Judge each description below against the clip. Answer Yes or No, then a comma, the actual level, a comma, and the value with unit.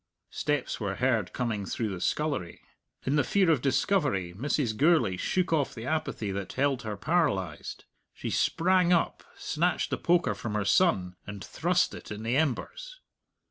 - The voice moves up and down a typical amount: No, wide, 7.9 semitones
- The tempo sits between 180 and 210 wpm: No, average, 165 wpm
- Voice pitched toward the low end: Yes, low, 130 Hz